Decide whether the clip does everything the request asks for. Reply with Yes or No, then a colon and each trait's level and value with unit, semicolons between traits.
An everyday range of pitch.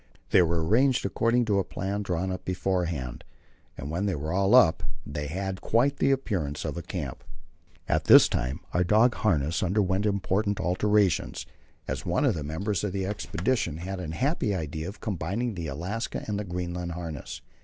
Yes: average, 4.0 semitones